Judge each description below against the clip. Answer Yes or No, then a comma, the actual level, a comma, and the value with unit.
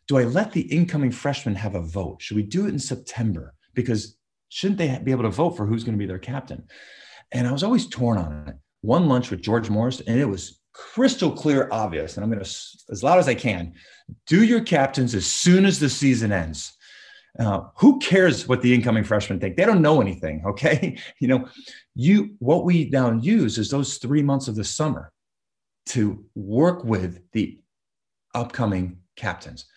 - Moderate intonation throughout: No, wide, 6.6 semitones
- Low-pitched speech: Yes, low, 125 Hz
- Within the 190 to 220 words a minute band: Yes, average, 200 wpm